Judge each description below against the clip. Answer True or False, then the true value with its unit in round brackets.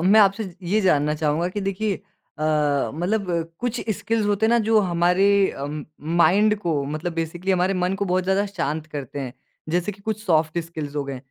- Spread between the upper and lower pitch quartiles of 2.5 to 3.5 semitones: False (4.2 semitones)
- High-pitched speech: False (180 Hz)